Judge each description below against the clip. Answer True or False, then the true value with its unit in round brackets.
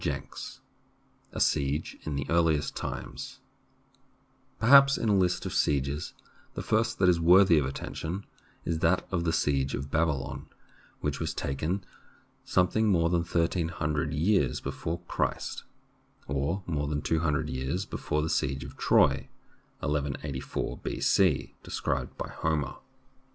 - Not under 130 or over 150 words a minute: True (135 wpm)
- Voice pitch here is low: True (80 Hz)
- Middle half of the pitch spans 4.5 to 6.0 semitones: False (3.8 semitones)